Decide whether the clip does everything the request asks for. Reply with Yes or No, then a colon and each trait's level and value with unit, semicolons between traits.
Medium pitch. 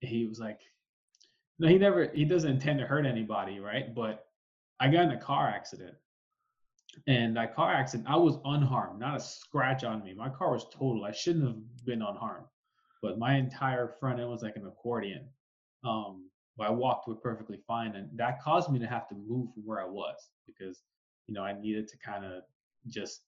No: low, 120 Hz